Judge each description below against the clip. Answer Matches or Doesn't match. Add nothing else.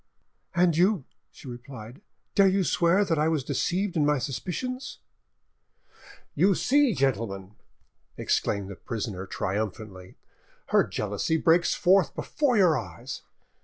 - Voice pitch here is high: Doesn't match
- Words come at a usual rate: Doesn't match